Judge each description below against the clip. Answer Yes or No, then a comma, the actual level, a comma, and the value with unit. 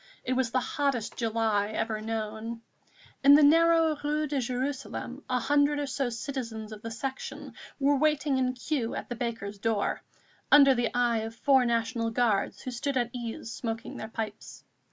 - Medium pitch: No, high, 245 Hz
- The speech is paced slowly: No, average, 175 wpm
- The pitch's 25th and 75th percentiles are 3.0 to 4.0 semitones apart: Yes, average, 3.6 semitones